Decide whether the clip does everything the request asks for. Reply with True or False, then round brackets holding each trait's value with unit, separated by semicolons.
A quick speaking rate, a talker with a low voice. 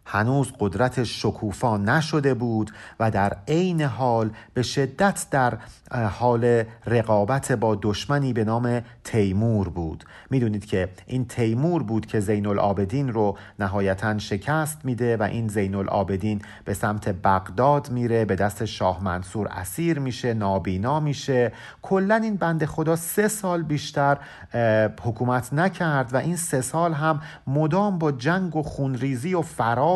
False (140 wpm; 120 Hz)